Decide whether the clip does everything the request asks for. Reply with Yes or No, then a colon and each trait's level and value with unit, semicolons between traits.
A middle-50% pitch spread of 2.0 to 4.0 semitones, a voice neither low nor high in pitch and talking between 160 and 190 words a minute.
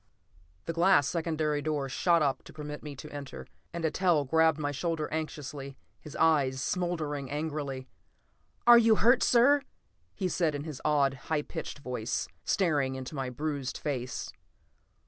No: average, 3.0 semitones; medium, 150 Hz; average, 145 wpm